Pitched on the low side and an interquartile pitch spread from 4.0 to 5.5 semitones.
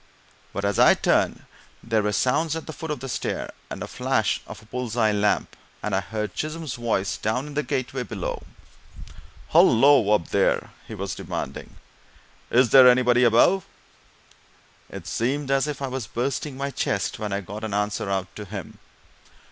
Yes: low, 120 Hz; average, 4.6 semitones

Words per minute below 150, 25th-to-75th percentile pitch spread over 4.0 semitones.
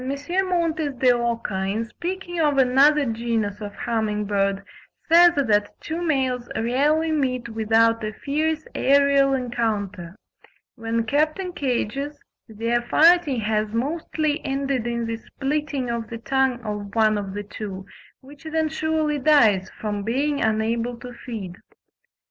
Yes: slow, 135 wpm; average, 5.0 semitones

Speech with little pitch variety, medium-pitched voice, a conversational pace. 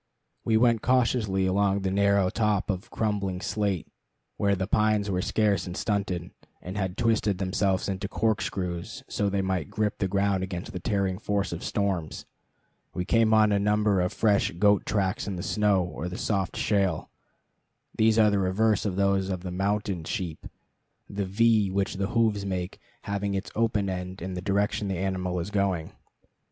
No: narrow, 2.0 semitones; low, 100 Hz; average, 175 wpm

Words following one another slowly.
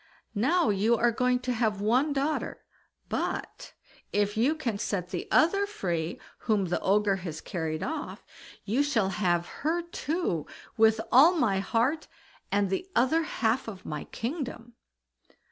No: average, 145 wpm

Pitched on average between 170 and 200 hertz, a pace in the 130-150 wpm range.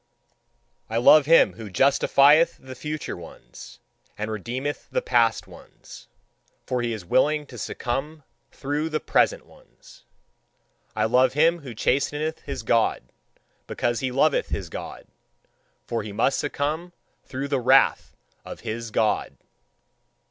No: low, 135 Hz; slow, 135 wpm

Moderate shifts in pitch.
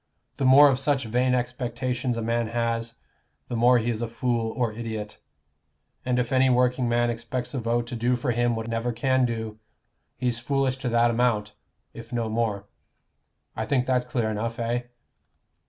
No: narrow, 1.5 semitones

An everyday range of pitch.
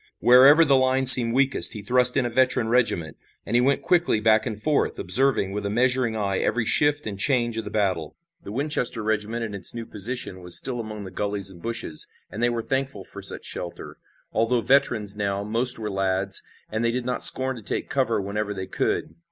Yes: average, 3.9 semitones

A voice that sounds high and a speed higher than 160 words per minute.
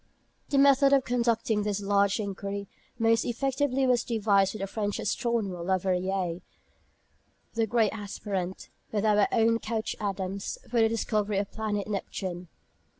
No: high, 210 Hz; average, 150 wpm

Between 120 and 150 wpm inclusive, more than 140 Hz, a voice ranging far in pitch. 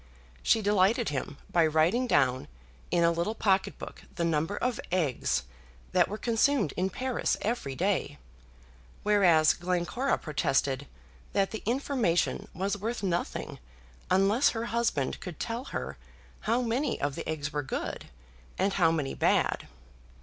Yes: average, 140 wpm; high, 190 Hz; wide, 6.2 semitones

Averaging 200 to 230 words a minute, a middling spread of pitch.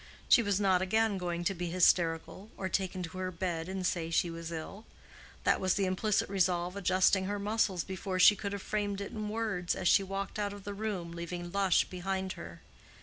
No: fast, 205 wpm; narrow, 2.3 semitones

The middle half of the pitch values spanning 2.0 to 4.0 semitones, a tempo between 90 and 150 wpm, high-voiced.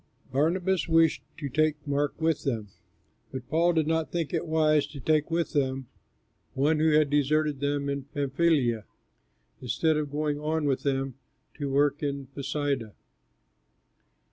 No: narrow, 2.4 semitones; average, 145 wpm; medium, 145 Hz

